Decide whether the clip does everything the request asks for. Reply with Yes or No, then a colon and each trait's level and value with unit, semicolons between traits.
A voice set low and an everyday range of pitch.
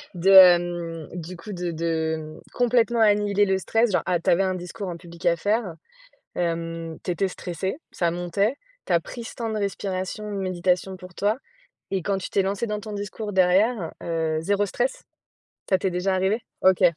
No: medium, 185 Hz; average, 3.1 semitones